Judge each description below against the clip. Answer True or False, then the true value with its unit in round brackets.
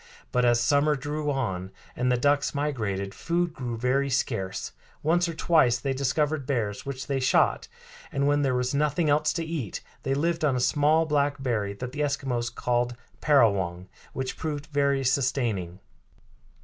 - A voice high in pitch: False (135 Hz)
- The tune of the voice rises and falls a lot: False (3.5 semitones)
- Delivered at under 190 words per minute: True (165 wpm)